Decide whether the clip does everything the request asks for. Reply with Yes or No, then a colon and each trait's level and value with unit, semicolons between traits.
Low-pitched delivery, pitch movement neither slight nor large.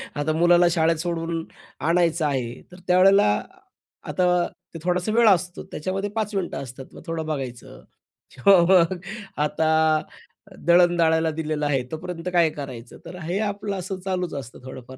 No: medium, 165 Hz; average, 3.1 semitones